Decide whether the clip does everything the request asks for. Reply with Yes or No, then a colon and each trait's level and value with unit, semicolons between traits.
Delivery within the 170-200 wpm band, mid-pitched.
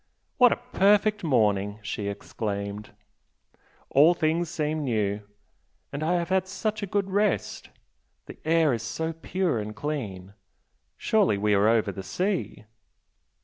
No: average, 140 wpm; medium, 155 Hz